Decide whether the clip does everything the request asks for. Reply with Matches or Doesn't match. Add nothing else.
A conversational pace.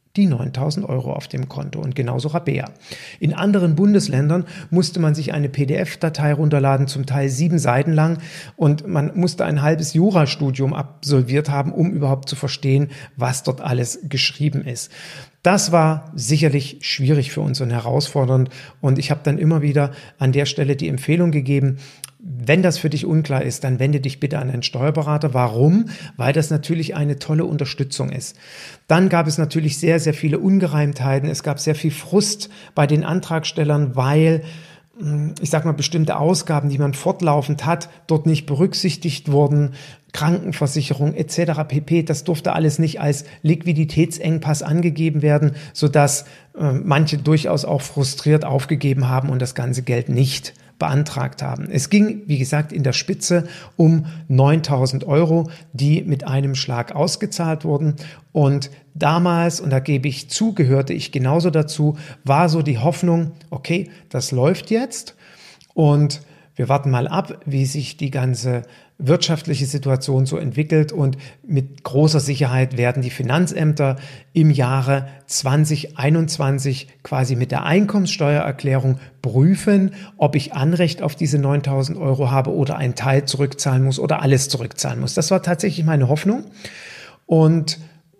Matches